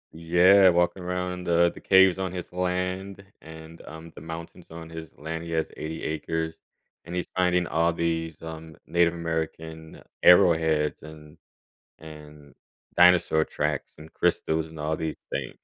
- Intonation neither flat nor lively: No, narrow, 1.9 semitones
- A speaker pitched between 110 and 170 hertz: No, very low, 80 Hz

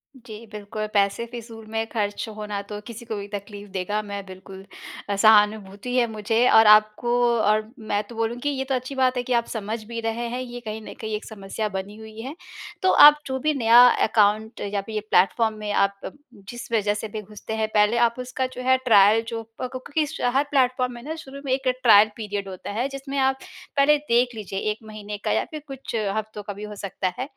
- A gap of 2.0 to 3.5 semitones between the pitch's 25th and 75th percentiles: Yes, average, 3.1 semitones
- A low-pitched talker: No, high, 220 Hz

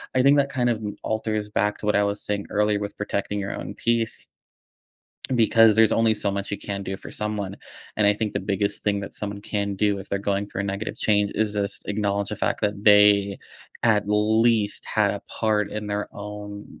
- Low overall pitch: Yes, low, 105 Hz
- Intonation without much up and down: Yes, narrow, 1.1 semitones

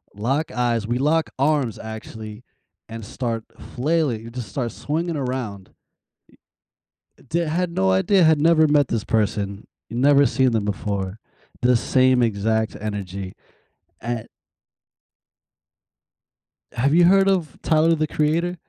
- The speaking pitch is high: No, low, 125 Hz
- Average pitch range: No, wide, 5.9 semitones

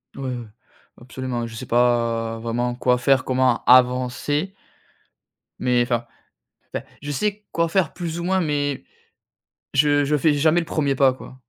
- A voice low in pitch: Yes, low, 130 Hz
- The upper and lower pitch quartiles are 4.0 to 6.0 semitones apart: No, average, 3.5 semitones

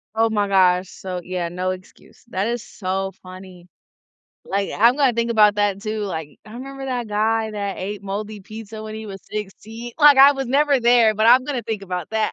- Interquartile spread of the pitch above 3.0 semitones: Yes, average, 3.4 semitones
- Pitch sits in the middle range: No, high, 215 Hz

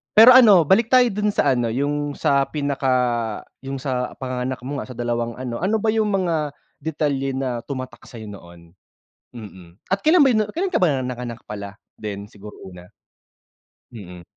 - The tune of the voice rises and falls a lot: Yes, wide, 5.7 semitones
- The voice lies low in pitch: Yes, low, 130 Hz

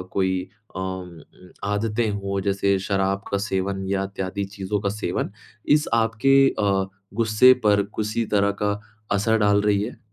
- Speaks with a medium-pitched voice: No, low, 100 Hz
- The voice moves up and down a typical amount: No, narrow, 1.7 semitones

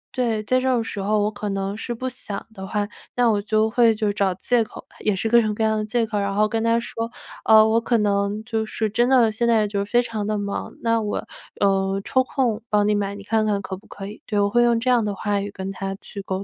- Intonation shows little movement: Yes, narrow, 2.2 semitones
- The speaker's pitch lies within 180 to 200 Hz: No, high, 215 Hz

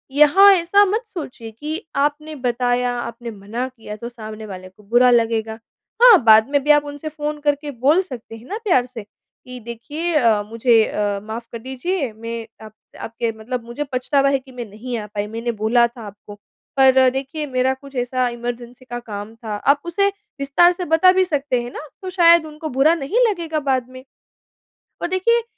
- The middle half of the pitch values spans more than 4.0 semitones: Yes, average, 4.8 semitones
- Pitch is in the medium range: No, very high, 255 Hz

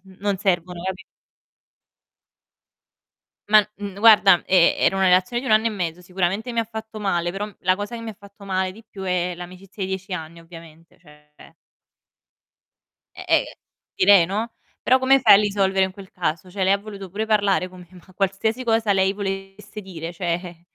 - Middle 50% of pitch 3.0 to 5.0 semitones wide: No, narrow, 2.5 semitones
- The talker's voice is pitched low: No, high, 195 Hz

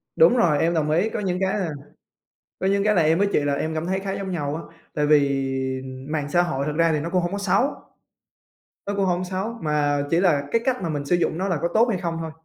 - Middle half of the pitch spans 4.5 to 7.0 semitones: No, average, 4.0 semitones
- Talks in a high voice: No, medium, 175 Hz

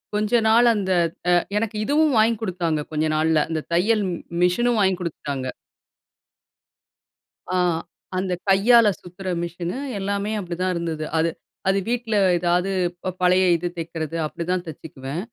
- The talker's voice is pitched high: No, medium, 180 Hz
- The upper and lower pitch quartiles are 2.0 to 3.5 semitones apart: No, average, 4.0 semitones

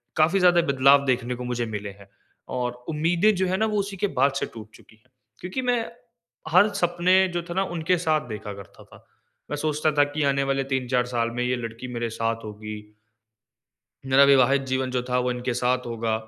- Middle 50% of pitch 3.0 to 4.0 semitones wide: No, average, 5.2 semitones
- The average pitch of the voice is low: Yes, low, 130 Hz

